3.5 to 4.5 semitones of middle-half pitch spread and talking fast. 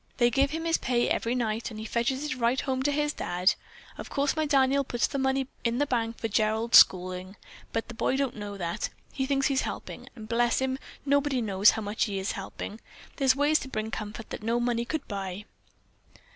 Yes: average, 4.0 semitones; fast, 215 wpm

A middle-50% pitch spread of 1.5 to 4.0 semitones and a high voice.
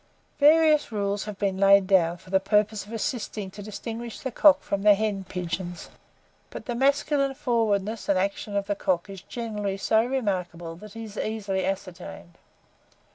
Yes: average, 3.0 semitones; high, 205 Hz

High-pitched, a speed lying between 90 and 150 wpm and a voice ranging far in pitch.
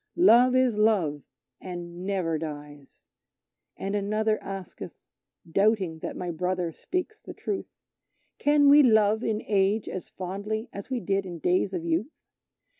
No: high, 195 Hz; average, 140 wpm; average, 3.9 semitones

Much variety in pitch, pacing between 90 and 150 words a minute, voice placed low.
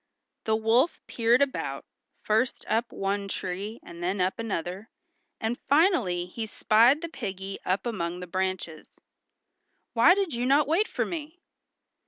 No: wide, 5.9 semitones; average, 145 wpm; high, 220 Hz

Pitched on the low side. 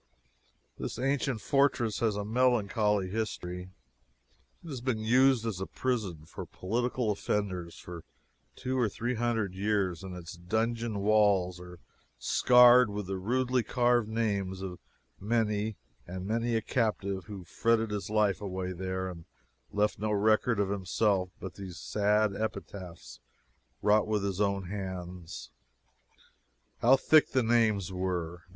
Yes: low, 105 Hz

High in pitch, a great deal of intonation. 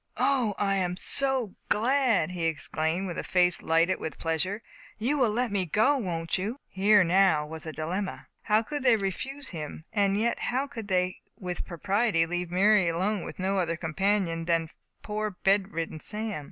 No: high, 195 Hz; average, 4.2 semitones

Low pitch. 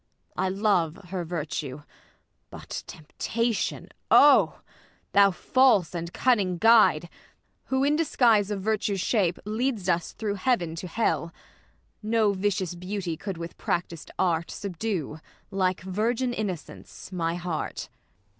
No: high, 190 Hz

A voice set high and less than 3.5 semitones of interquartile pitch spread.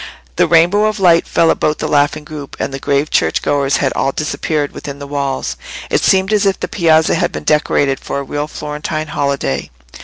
No: medium, 150 Hz; average, 2.7 semitones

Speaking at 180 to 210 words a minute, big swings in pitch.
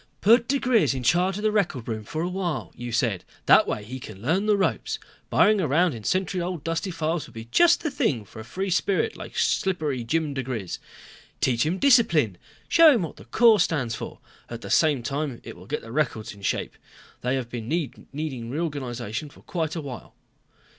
Yes: average, 200 wpm; wide, 7.5 semitones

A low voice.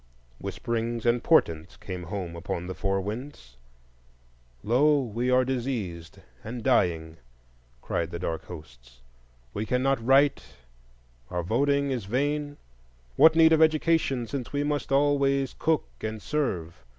Yes: low, 120 Hz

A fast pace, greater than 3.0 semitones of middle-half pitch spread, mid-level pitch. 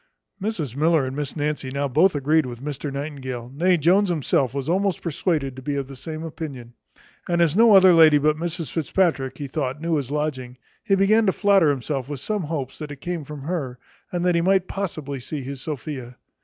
Yes: fast, 210 wpm; average, 4.0 semitones; medium, 150 Hz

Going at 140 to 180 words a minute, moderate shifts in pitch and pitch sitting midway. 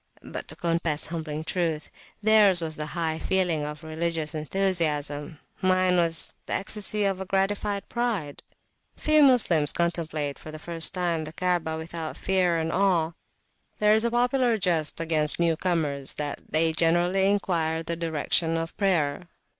Yes: average, 150 wpm; average, 3.3 semitones; medium, 170 Hz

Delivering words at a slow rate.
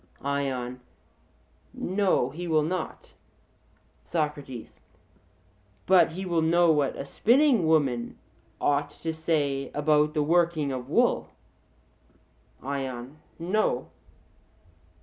Yes: slow, 95 wpm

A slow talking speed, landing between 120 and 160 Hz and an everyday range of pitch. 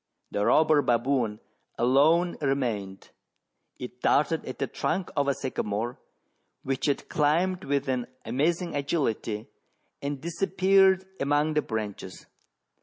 Yes: slow, 115 wpm; medium, 140 Hz; average, 4.7 semitones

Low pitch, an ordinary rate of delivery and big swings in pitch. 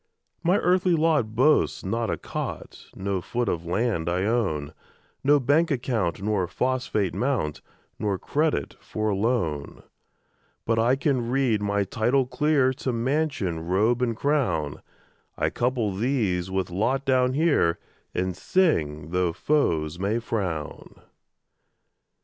No: low, 115 Hz; slow, 130 wpm; wide, 6.5 semitones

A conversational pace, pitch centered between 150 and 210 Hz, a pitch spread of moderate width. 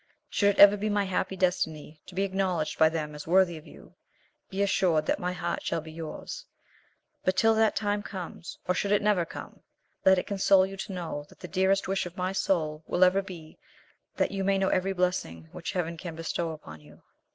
No: fast, 215 wpm; medium, 185 Hz; average, 3.2 semitones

